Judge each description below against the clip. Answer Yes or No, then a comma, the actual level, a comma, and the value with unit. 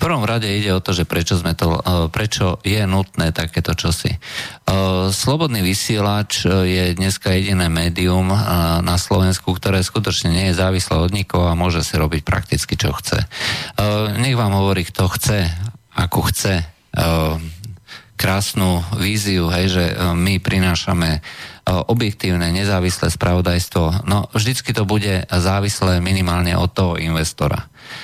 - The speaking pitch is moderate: No, very low, 95 Hz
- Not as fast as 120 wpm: No, average, 130 wpm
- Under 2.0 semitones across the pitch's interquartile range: No, narrow, 2.6 semitones